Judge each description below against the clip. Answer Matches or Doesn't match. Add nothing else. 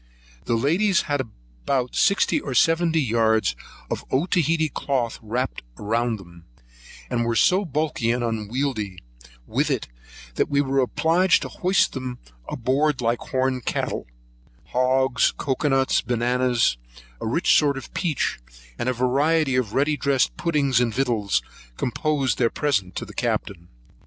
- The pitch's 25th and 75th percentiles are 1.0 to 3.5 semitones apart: Doesn't match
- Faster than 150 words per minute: Doesn't match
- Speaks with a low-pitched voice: Matches